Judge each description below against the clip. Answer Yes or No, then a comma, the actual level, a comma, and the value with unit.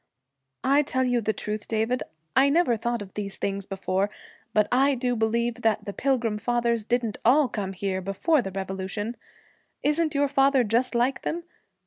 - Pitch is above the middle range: Yes, high, 235 Hz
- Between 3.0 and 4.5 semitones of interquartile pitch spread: Yes, average, 4.1 semitones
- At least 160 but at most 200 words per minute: Yes, average, 170 wpm